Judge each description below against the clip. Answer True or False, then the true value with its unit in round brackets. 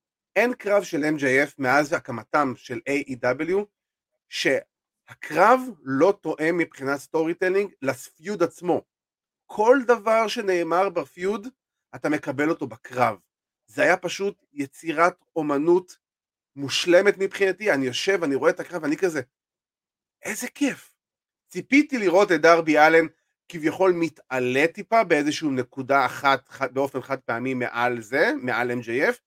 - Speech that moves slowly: False (120 wpm)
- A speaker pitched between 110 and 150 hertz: False (165 Hz)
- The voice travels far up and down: True (6.0 semitones)